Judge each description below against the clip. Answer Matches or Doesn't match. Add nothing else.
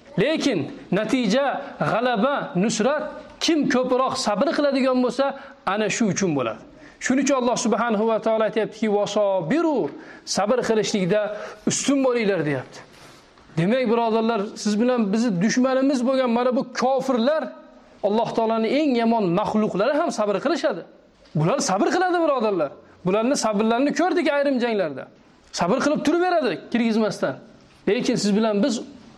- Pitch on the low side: Doesn't match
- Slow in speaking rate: Matches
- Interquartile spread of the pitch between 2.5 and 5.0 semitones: Matches